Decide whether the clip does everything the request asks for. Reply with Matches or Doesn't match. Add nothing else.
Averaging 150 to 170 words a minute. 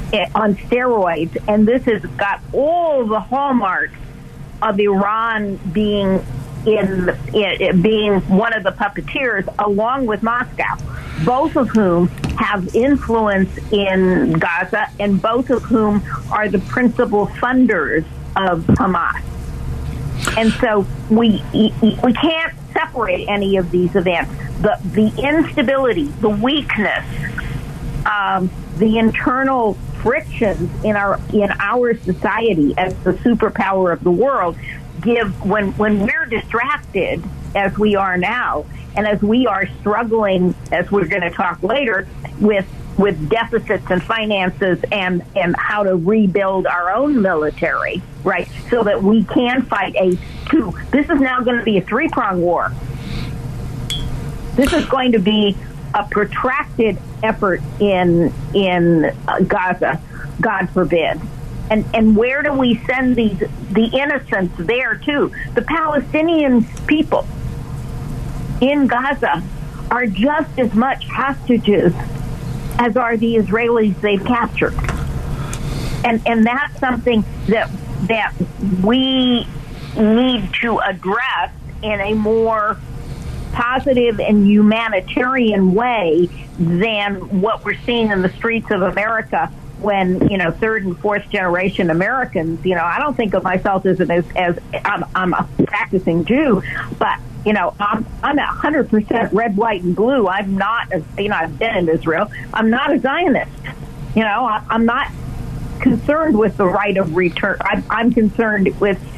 Doesn't match